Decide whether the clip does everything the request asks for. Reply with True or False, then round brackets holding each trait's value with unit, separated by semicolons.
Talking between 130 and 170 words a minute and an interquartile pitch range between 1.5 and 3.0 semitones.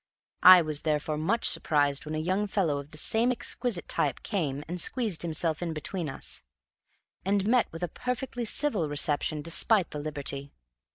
False (165 wpm; 5.4 semitones)